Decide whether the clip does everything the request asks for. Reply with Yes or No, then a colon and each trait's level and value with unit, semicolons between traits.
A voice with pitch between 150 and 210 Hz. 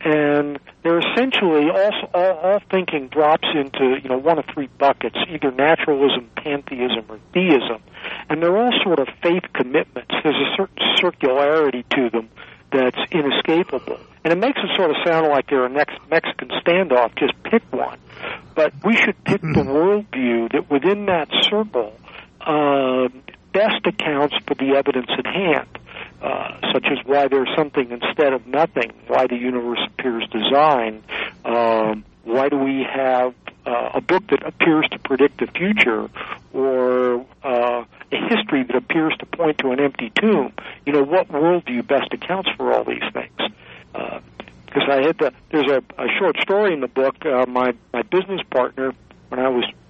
No: medium, 140 Hz